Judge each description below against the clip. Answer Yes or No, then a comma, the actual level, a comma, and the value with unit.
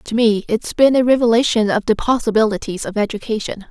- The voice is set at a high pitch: Yes, high, 220 Hz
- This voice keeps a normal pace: Yes, average, 180 wpm